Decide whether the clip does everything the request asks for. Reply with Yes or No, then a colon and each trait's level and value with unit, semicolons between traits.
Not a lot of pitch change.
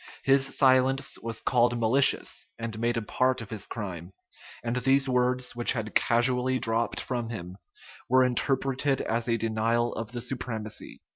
Yes: narrow, 2.3 semitones